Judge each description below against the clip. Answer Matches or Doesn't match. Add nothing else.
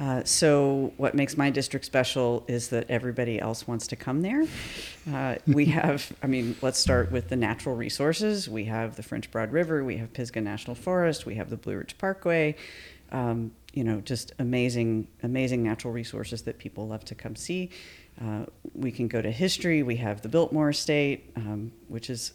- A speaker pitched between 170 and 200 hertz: Doesn't match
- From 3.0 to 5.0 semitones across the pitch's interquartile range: Matches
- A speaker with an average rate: Matches